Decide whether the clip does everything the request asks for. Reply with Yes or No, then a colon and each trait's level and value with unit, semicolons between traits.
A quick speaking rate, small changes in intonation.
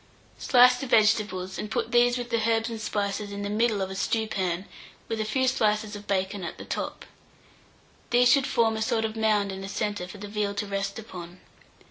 Yes: fast, 210 wpm; narrow, 2.2 semitones